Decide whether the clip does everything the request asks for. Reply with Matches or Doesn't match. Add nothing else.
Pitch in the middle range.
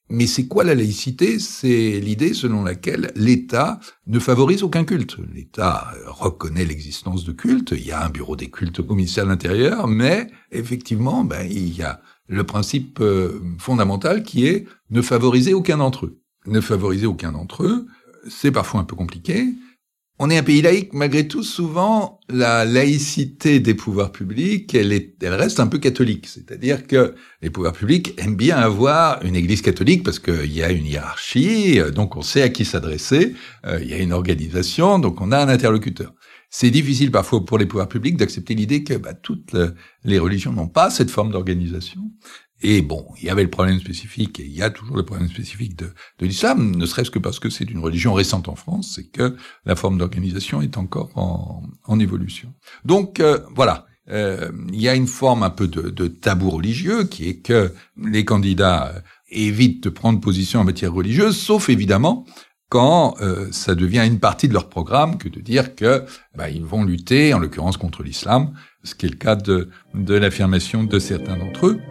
Doesn't match